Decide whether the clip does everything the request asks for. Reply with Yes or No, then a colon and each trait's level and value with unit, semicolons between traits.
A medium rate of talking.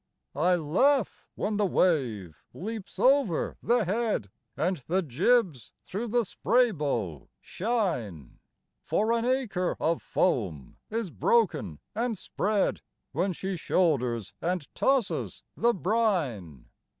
No: slow, 115 wpm